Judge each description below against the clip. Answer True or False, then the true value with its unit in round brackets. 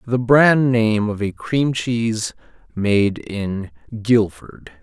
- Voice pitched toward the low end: True (110 Hz)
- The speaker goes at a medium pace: False (125 wpm)